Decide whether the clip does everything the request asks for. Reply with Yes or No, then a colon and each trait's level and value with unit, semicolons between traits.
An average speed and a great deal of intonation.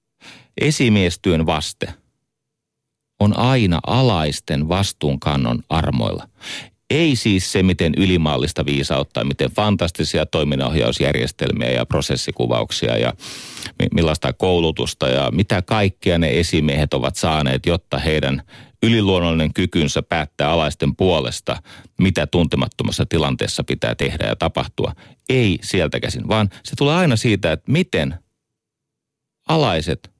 Yes: average, 105 wpm; wide, 6.1 semitones